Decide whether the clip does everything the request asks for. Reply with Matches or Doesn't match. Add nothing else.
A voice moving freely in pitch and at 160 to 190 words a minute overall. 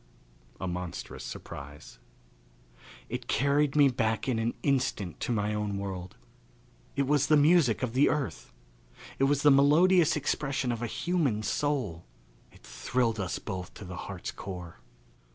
Doesn't match